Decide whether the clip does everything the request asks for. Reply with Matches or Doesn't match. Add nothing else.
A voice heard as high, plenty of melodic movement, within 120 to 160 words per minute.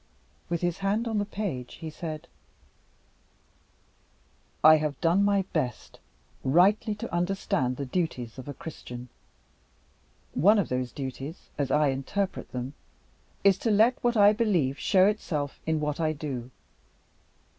Doesn't match